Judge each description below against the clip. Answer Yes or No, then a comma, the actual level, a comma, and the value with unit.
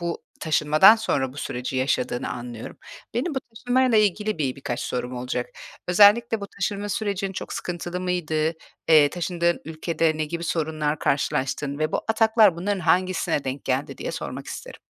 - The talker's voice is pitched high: No, medium, 170 Hz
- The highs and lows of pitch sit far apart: Yes, wide, 5.9 semitones